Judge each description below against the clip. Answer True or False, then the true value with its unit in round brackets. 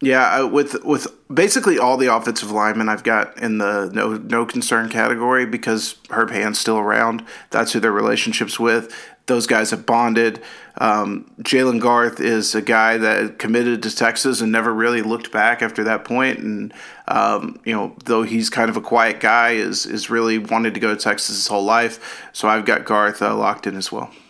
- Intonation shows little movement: True (1.5 semitones)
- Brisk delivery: False (195 wpm)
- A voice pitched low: True (115 Hz)